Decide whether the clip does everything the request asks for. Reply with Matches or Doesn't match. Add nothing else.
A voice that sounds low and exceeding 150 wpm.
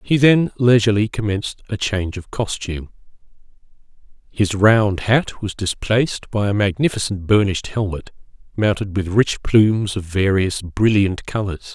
Doesn't match